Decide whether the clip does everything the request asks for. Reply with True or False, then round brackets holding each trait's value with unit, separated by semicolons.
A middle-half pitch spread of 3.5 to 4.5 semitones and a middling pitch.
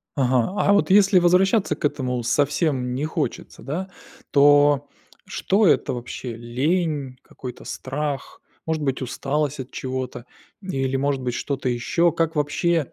True (4.0 semitones; 145 Hz)